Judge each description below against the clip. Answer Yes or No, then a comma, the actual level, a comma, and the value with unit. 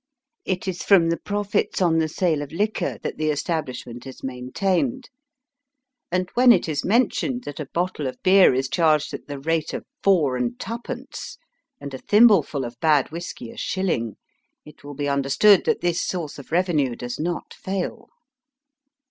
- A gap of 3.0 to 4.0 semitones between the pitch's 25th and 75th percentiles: No, average, 5.3 semitones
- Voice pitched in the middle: Yes, medium, 165 Hz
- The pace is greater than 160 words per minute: Yes, average, 170 wpm